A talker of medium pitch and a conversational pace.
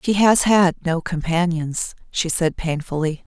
Yes: medium, 170 Hz; average, 145 wpm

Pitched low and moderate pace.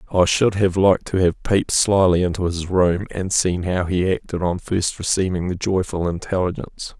Yes: very low, 90 Hz; average, 190 wpm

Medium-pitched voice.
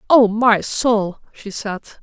No: high, 220 Hz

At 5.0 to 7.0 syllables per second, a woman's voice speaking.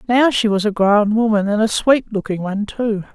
Yes: 5.3 syllables/s; female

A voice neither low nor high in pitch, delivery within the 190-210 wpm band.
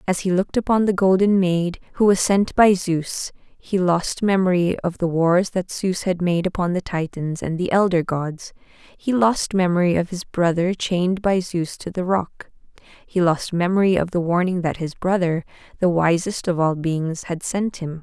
Yes: medium, 180 Hz; average, 195 wpm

